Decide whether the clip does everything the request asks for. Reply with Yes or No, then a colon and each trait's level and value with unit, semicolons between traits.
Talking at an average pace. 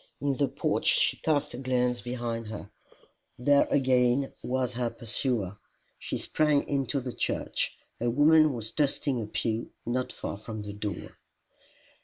Yes: average, 150 wpm